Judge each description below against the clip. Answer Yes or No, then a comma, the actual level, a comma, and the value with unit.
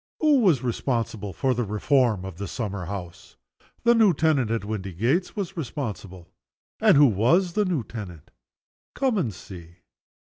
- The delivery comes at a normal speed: Yes, average, 155 wpm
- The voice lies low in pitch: Yes, low, 115 Hz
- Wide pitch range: Yes, wide, 8.8 semitones